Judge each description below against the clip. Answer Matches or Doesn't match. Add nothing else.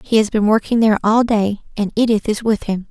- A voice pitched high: Matches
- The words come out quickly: Matches